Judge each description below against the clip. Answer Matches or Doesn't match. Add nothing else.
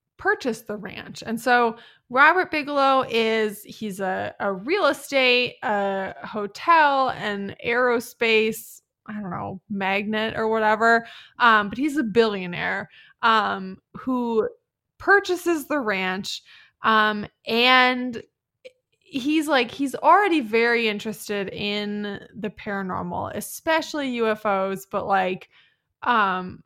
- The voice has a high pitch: Matches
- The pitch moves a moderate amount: Matches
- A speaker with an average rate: Doesn't match